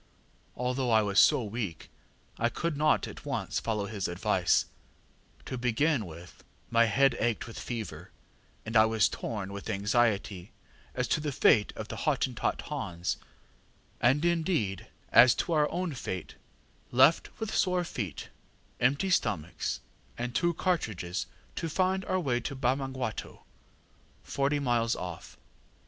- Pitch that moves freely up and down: Yes, wide, 5.7 semitones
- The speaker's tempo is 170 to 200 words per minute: No, average, 140 wpm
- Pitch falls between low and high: No, low, 120 Hz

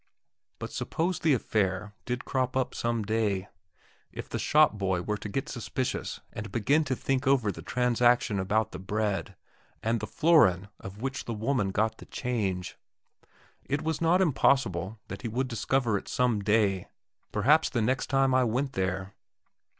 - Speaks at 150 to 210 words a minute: Yes, average, 165 wpm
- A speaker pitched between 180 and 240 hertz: No, low, 115 Hz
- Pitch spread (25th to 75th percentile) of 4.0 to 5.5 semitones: Yes, average, 4.6 semitones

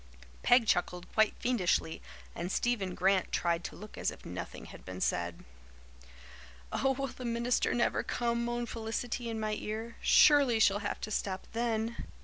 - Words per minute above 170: No, average, 160 wpm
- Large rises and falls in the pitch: No, average, 4.0 semitones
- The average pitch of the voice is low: No, high, 225 Hz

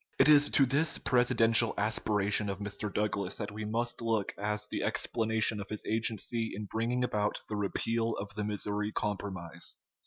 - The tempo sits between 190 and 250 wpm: No, average, 165 wpm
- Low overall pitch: Yes, low, 105 Hz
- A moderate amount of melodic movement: No, narrow, 1.9 semitones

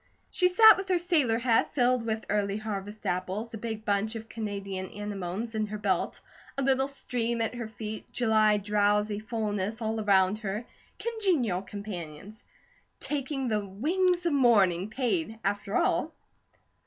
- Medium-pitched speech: No, high, 220 Hz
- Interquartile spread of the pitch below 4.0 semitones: Yes, average, 3.4 semitones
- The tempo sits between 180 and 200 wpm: No, average, 150 wpm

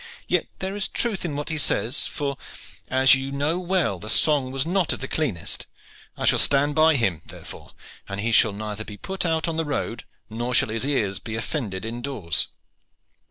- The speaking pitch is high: No, low, 135 Hz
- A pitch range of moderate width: No, wide, 6.2 semitones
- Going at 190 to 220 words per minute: Yes, average, 195 wpm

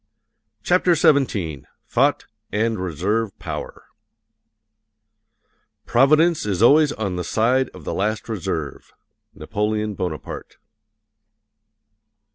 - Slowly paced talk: Yes, slow, 85 wpm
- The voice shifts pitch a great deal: Yes, wide, 6.0 semitones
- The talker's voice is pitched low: Yes, low, 110 Hz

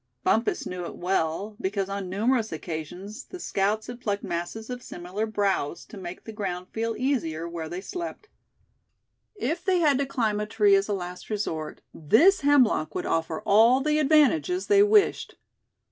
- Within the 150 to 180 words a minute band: Yes, average, 170 wpm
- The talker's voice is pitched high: Yes, high, 210 Hz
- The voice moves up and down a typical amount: No, wide, 6.6 semitones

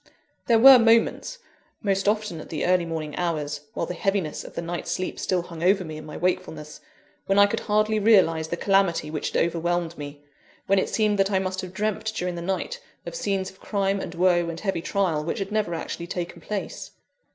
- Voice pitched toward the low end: No, medium, 185 Hz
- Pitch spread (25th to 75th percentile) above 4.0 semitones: No, average, 3.2 semitones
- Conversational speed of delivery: No, fast, 210 wpm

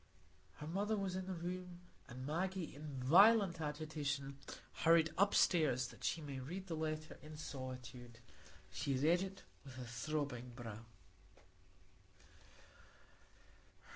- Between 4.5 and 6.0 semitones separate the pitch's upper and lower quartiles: Yes, average, 5.2 semitones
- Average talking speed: No, slow, 120 wpm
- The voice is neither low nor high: Yes, medium, 155 Hz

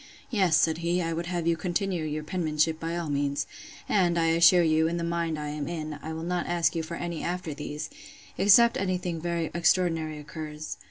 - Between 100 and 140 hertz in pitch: No, medium, 165 Hz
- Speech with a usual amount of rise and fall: No, narrow, 1.8 semitones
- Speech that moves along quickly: Yes, fast, 210 wpm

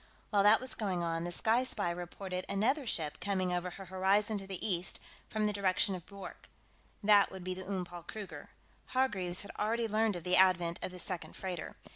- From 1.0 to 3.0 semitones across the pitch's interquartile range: Yes, average, 2.7 semitones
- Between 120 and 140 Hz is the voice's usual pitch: No, high, 190 Hz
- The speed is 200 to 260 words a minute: Yes, fast, 205 wpm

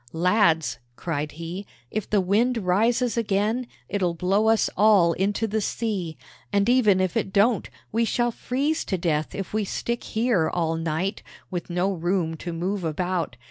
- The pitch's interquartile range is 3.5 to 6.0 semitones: Yes, average, 4.4 semitones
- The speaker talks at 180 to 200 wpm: No, average, 165 wpm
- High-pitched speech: Yes, high, 195 Hz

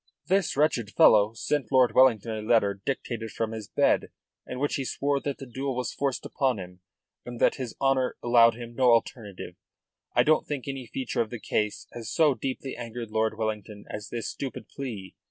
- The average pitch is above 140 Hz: No, low, 120 Hz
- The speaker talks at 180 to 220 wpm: Yes, average, 190 wpm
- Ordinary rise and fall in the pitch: Yes, average, 3.5 semitones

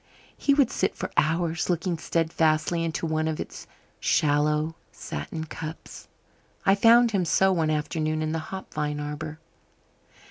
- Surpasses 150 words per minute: No, average, 145 wpm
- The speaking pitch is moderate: Yes, medium, 160 Hz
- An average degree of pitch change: No, narrow, 2.0 semitones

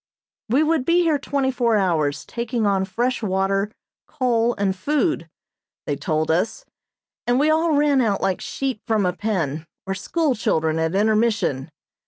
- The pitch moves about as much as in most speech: No, wide, 6.0 semitones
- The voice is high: Yes, high, 215 Hz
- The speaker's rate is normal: Yes, average, 160 wpm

